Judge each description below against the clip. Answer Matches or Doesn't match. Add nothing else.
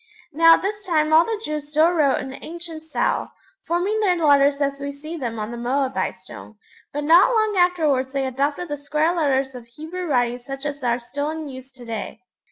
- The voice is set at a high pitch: Matches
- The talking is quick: Matches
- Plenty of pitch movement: Doesn't match